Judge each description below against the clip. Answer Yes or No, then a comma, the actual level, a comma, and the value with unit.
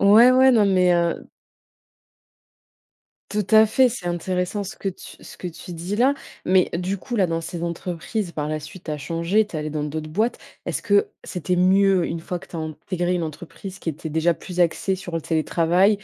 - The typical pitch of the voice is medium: Yes, medium, 180 Hz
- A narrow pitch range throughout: No, average, 3.2 semitones